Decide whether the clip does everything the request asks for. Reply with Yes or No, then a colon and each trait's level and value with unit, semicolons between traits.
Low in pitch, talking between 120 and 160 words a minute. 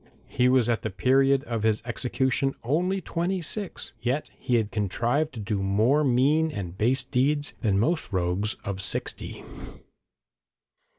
Yes: low, 125 Hz; average, 145 wpm